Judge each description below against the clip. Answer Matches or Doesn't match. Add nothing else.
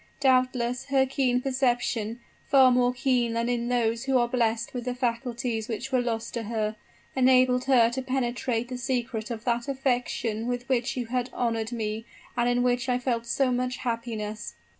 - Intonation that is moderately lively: Doesn't match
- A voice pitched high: Matches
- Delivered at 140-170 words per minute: Doesn't match